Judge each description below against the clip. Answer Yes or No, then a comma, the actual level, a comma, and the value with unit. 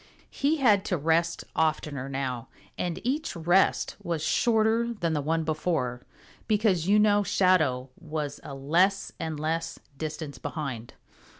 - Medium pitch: Yes, medium, 165 Hz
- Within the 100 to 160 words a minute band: Yes, slow, 135 wpm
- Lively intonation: No, average, 4.8 semitones